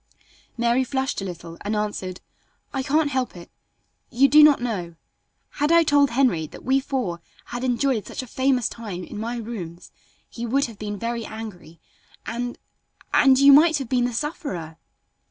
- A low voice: No, high, 240 Hz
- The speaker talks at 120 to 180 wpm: Yes, average, 170 wpm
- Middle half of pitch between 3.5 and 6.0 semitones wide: Yes, average, 4.8 semitones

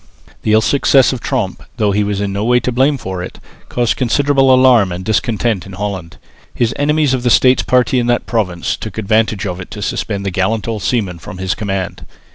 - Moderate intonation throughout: Yes, average, 4.1 semitones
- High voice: No, low, 110 Hz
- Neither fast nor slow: No, fast, 215 wpm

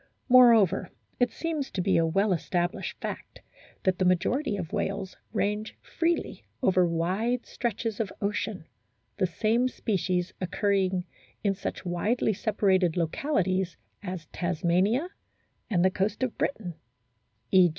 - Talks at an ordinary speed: No, slow, 130 wpm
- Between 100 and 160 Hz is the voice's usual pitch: No, high, 195 Hz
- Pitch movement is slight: No, average, 3.7 semitones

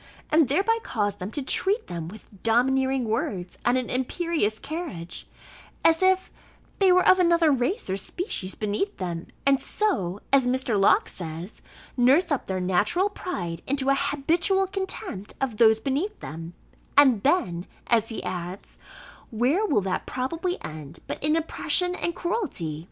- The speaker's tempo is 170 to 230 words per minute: No, average, 155 wpm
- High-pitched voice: Yes, very high, 260 Hz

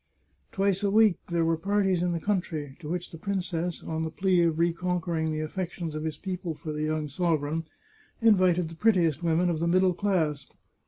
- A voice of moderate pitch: Yes, medium, 170 Hz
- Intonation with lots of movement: No, average, 2.7 semitones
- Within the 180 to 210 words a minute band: Yes, fast, 205 wpm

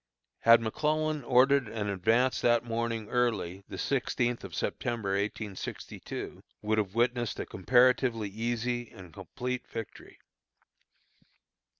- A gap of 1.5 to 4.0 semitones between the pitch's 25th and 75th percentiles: Yes, narrow, 2.6 semitones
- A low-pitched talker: Yes, low, 115 Hz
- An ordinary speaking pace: No, slow, 110 wpm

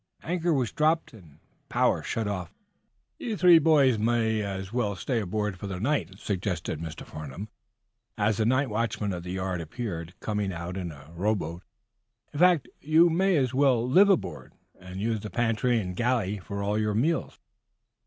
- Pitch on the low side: Yes, low, 105 Hz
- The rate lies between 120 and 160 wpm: No, average, 185 wpm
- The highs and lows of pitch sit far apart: Yes, wide, 5.7 semitones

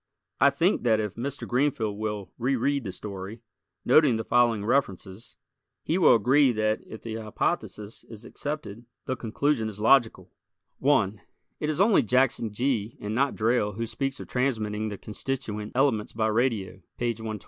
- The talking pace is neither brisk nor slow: Yes, average, 160 wpm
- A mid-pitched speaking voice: No, low, 115 Hz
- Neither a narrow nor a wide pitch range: Yes, average, 3.9 semitones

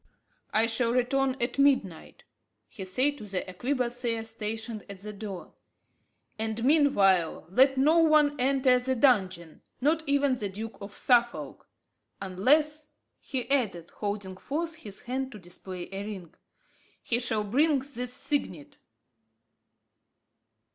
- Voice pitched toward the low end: No, high, 235 Hz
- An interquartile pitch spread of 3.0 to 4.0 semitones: No, average, 5.2 semitones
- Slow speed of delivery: Yes, slow, 125 wpm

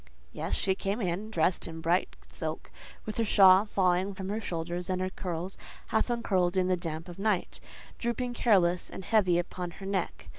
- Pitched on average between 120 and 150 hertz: No, medium, 185 Hz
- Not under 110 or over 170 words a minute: No, average, 185 wpm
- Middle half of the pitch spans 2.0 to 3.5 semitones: Yes, narrow, 2.6 semitones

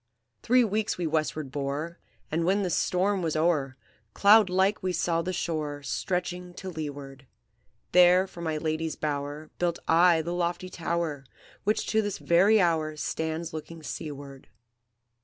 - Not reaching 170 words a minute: Yes, average, 150 wpm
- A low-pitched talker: No, medium, 170 Hz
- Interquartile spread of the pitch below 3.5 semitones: Yes, average, 2.8 semitones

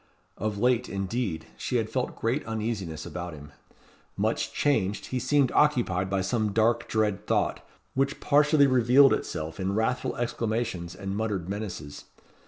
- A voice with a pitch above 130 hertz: No, low, 110 Hz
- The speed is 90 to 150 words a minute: Yes, average, 145 wpm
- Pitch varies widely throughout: No, average, 4.7 semitones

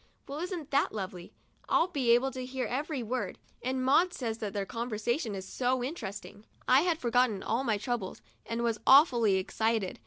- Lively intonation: No, average, 3.7 semitones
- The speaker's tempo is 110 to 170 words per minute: No, average, 180 wpm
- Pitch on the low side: No, high, 245 Hz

